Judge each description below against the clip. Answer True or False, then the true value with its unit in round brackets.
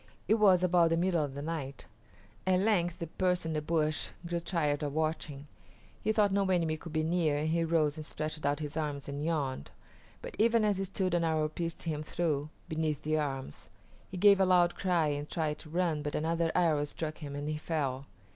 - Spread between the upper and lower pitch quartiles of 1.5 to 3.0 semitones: True (2.6 semitones)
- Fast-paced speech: True (215 wpm)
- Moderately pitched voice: True (160 Hz)